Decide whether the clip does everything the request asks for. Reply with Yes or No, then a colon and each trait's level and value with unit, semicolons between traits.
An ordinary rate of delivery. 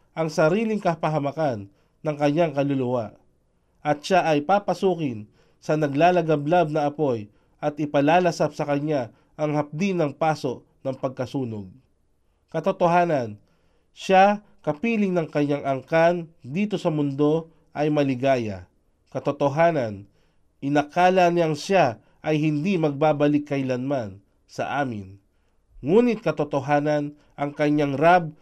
No: slow, 105 wpm